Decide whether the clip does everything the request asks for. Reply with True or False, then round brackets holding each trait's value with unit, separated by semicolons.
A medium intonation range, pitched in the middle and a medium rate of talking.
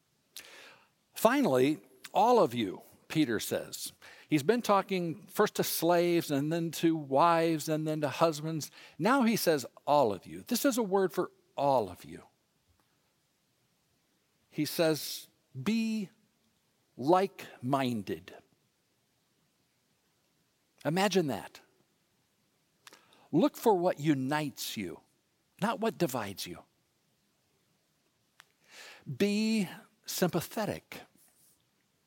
False (4.8 semitones; 170 Hz; 95 wpm)